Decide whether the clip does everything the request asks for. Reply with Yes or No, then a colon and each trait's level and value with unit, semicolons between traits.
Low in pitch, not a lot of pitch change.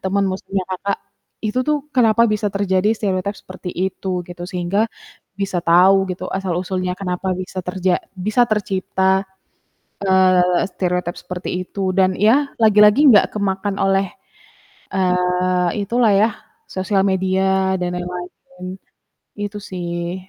No: high, 190 Hz; narrow, 1.8 semitones